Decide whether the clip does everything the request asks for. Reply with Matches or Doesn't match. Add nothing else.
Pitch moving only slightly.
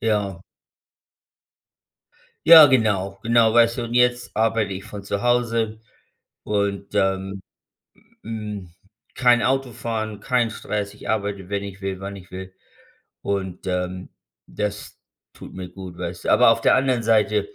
Doesn't match